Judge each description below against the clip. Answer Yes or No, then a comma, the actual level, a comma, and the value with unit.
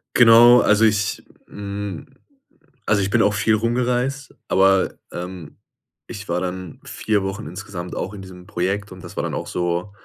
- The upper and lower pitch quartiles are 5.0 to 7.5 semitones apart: No, average, 2.9 semitones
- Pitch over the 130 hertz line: No, low, 100 Hz